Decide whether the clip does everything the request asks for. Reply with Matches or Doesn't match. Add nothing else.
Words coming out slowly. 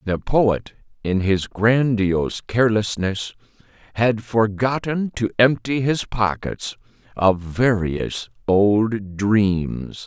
Matches